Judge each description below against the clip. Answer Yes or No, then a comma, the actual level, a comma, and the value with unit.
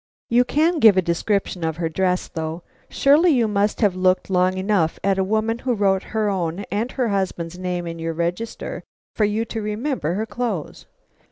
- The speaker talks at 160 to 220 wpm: Yes, average, 190 wpm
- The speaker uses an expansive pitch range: No, average, 4.0 semitones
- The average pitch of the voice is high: Yes, high, 195 Hz